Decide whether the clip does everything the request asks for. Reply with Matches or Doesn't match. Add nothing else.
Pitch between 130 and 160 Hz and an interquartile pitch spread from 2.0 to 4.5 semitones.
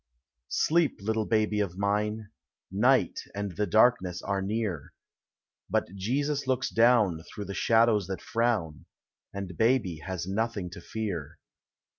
Doesn't match